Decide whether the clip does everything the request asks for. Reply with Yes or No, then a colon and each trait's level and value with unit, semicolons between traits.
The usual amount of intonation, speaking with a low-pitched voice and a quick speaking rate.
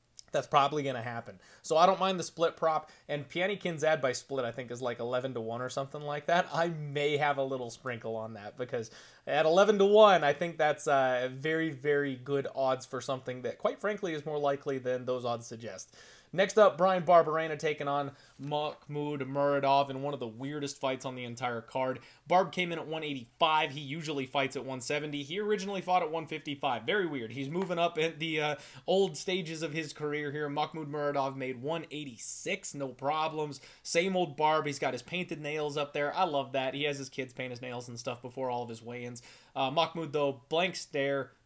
No: average, 3.5 semitones; medium, 145 Hz; fast, 215 wpm